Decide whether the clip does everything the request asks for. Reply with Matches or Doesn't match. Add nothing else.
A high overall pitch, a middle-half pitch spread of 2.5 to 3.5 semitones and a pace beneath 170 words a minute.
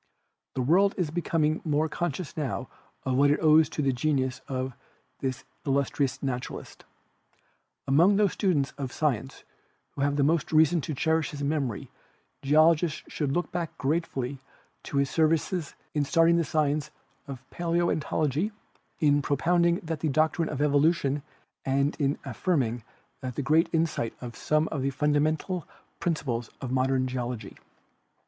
Doesn't match